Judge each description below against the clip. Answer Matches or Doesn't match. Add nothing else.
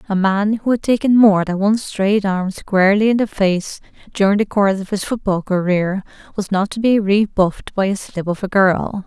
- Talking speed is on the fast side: Matches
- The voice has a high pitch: Matches